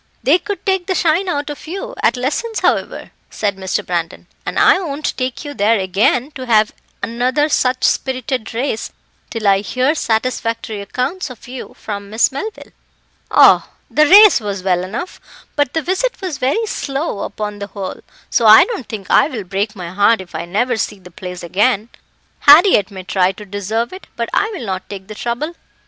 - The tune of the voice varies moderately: No, wide, 6.5 semitones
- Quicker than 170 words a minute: Yes, average, 190 wpm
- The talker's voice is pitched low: No, high, 235 Hz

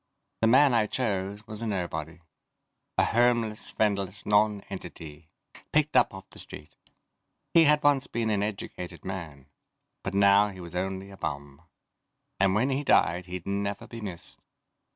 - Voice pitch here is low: Yes, low, 100 Hz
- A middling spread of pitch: Yes, average, 3.6 semitones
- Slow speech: No, average, 155 wpm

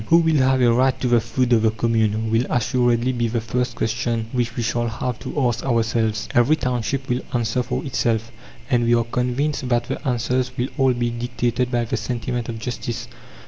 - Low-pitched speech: Yes, low, 120 Hz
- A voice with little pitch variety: Yes, narrow, 1.6 semitones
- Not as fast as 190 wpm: No, fast, 205 wpm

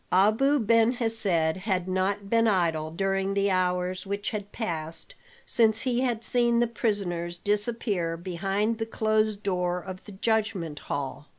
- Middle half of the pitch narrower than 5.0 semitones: Yes, average, 3.7 semitones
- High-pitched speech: Yes, high, 200 Hz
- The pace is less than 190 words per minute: Yes, average, 150 wpm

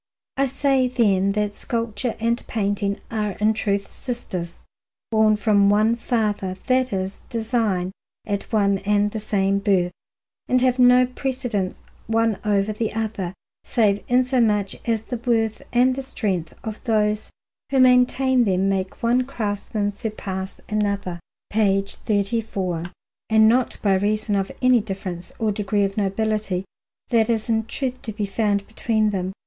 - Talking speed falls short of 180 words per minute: Yes, average, 145 wpm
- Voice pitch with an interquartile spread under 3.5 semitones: Yes, average, 2.8 semitones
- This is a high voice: Yes, high, 215 Hz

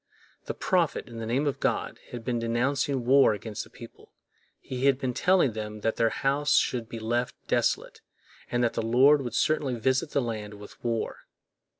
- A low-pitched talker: Yes, low, 120 Hz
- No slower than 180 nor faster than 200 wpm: Yes, average, 190 wpm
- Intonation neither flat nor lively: Yes, average, 3.1 semitones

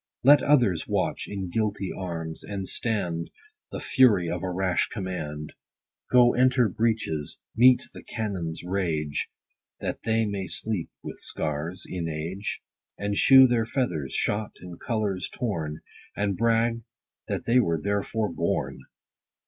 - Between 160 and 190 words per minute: No, average, 140 wpm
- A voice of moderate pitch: No, low, 100 Hz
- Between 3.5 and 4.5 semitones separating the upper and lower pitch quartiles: No, average, 5.0 semitones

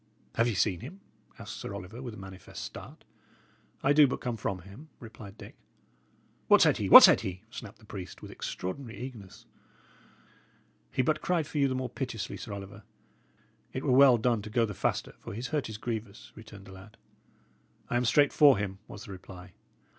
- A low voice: Yes, low, 110 Hz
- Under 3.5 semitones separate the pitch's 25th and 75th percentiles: No, average, 4.5 semitones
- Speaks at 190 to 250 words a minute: Yes, average, 195 wpm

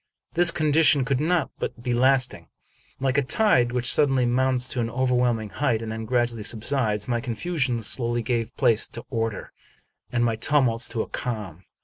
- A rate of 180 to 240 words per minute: No, average, 165 wpm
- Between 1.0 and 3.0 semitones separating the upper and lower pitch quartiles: Yes, average, 2.7 semitones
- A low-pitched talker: Yes, low, 125 Hz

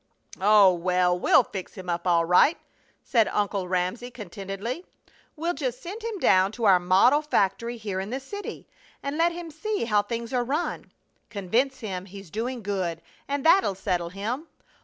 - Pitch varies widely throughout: Yes, wide, 6.4 semitones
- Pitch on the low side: No, high, 215 Hz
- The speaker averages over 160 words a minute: Yes, average, 170 wpm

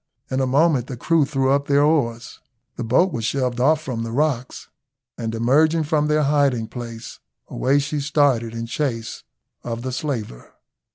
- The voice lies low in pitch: Yes, low, 130 Hz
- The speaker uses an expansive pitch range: No, average, 4.0 semitones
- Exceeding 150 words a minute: Yes, average, 170 wpm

